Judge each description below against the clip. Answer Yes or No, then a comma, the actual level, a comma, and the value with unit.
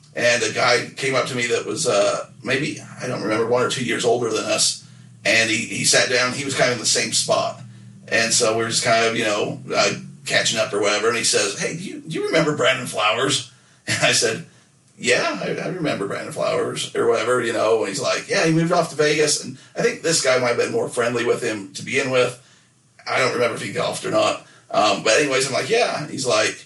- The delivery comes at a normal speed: No, fast, 250 wpm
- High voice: No, low, 135 Hz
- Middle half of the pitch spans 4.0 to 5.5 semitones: Yes, average, 4.8 semitones